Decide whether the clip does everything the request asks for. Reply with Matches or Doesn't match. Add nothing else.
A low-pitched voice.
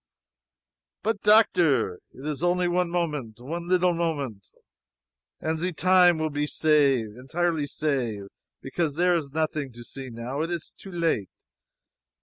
Doesn't match